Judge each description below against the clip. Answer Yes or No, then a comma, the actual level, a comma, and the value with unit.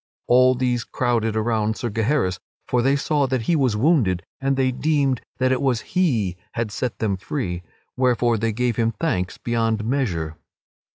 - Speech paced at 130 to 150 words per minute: No, average, 170 wpm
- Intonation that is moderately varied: Yes, average, 3.2 semitones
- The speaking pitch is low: Yes, low, 120 Hz